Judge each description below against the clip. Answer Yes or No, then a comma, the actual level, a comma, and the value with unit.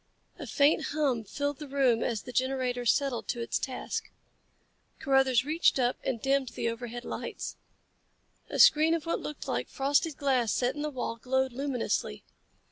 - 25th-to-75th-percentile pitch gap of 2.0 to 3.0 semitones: Yes, average, 2.7 semitones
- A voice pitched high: Yes, very high, 265 Hz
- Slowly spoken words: No, average, 165 wpm